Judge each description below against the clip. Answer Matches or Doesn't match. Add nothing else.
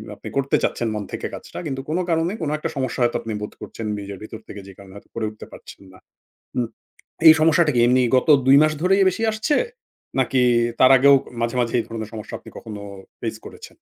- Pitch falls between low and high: Doesn't match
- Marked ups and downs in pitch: Matches